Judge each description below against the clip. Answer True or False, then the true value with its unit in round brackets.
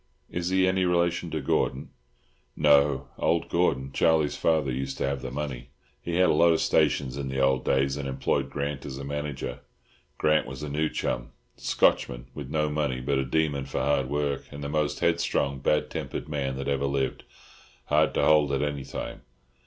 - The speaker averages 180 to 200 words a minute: True (185 wpm)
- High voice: False (70 Hz)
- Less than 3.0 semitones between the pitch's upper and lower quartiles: True (2.4 semitones)